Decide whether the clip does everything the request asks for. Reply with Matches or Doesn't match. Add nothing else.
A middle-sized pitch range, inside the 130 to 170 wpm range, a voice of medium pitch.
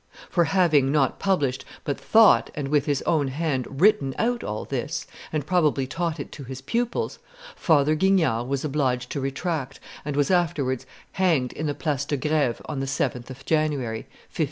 Doesn't match